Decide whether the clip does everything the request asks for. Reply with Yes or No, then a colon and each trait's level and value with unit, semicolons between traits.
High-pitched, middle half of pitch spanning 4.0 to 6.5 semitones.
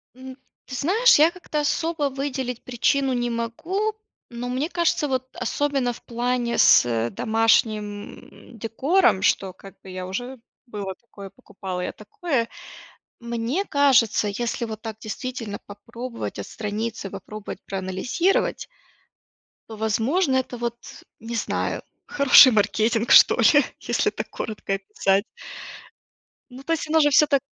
Yes: high, 235 Hz; average, 4.6 semitones